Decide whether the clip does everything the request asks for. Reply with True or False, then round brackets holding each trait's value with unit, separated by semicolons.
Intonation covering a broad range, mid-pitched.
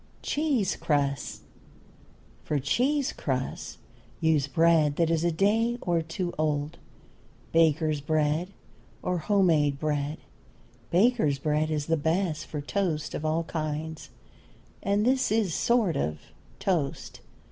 False (4.3 semitones; 160 Hz)